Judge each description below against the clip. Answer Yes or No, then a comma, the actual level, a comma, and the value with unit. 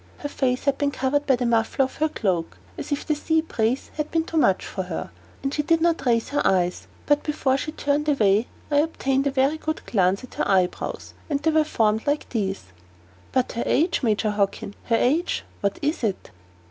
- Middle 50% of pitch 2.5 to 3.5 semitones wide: No, wide, 5.4 semitones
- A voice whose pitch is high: Yes, very high, 265 Hz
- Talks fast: Yes, fast, 210 wpm